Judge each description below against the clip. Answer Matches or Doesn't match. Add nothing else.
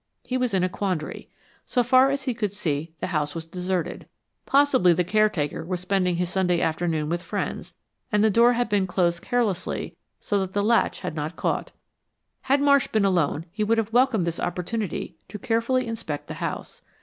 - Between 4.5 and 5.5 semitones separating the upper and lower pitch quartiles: Matches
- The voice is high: Matches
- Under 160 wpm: Doesn't match